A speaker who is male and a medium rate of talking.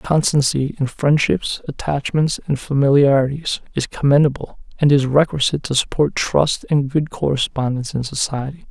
No: male; slow, 130 wpm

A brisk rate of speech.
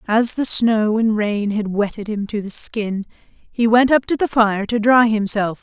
Yes: fast, 215 wpm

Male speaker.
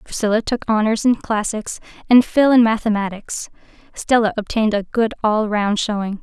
No: female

